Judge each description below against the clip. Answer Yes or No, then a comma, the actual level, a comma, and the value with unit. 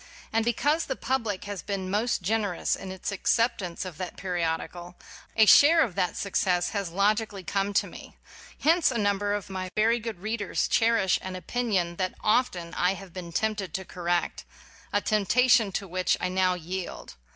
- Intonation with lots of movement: No, average, 3.5 semitones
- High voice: Yes, high, 195 Hz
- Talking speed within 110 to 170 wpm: No, average, 180 wpm